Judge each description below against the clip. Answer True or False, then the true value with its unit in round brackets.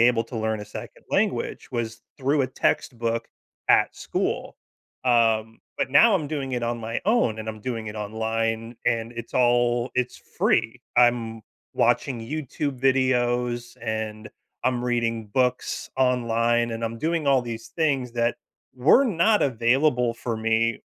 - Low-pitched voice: True (120 Hz)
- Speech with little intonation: True (2.2 semitones)